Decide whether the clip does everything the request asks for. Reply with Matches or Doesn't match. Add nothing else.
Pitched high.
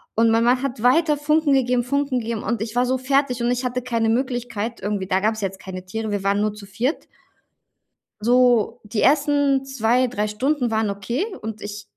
Matches